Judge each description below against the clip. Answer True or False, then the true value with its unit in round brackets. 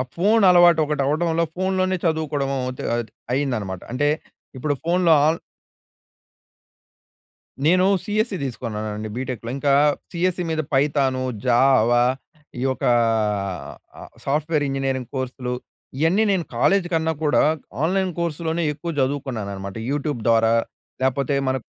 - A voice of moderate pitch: True (145 Hz)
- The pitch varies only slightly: False (4.9 semitones)